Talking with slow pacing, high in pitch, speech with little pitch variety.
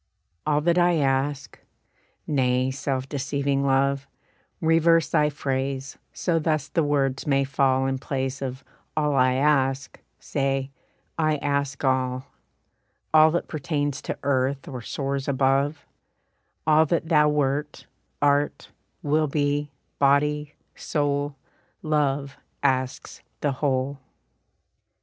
No: slow, 115 wpm; medium, 140 Hz; narrow, 1.8 semitones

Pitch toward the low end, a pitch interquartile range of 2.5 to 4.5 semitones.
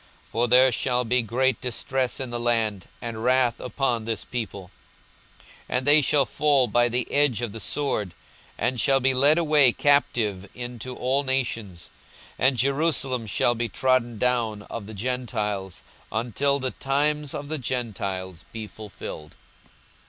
Yes: low, 125 Hz; average, 3.2 semitones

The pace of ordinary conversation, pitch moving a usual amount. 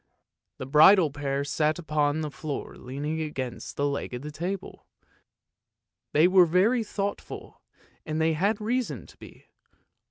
Yes: average, 150 wpm; average, 4.2 semitones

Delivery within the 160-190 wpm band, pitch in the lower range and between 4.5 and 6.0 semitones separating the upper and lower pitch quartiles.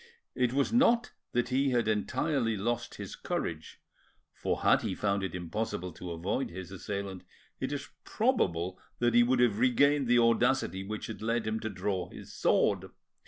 Yes: average, 170 wpm; low, 115 Hz; average, 4.9 semitones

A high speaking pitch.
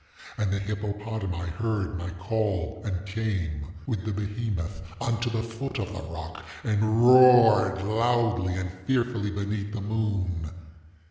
No: low, 105 Hz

